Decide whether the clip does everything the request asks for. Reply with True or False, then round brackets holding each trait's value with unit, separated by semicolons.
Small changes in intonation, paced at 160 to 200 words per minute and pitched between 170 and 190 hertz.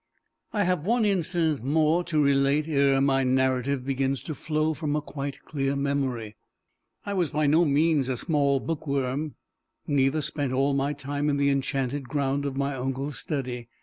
False (2.2 semitones; 170 wpm; 140 Hz)